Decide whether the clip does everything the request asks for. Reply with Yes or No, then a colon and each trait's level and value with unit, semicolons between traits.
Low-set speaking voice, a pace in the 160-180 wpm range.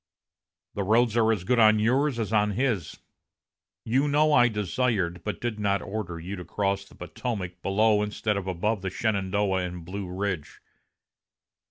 Yes: low, 105 Hz; average, 165 wpm